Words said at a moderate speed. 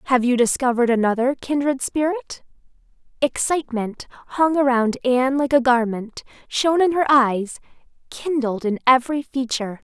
No: slow, 125 wpm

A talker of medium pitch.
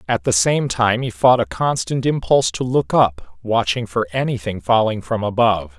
No: low, 110 Hz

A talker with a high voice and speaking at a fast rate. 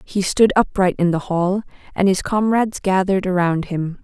No: high, 195 Hz; average, 180 wpm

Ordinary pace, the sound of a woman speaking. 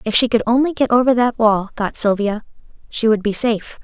No: fast, 220 wpm; female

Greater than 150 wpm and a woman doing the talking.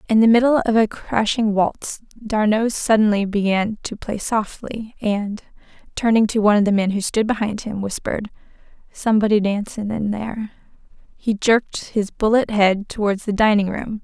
Yes: average, 160 wpm; female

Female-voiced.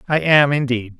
No: male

